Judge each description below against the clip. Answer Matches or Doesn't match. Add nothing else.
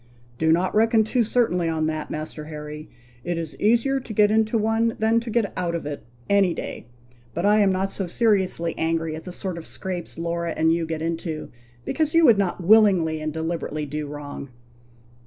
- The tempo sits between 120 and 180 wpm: Doesn't match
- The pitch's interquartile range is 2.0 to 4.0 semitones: Doesn't match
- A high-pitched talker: Doesn't match